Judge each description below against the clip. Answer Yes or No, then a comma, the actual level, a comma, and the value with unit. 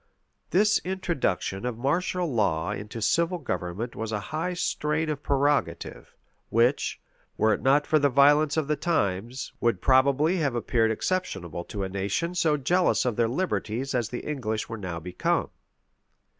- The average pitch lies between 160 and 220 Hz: No, low, 130 Hz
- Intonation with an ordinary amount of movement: No, wide, 6.3 semitones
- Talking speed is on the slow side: No, average, 155 wpm